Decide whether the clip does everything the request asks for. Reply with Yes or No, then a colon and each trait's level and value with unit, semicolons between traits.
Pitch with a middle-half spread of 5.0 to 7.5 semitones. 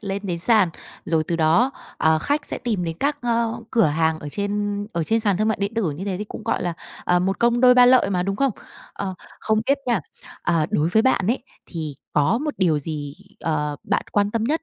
Yes: wide, 5.6 semitones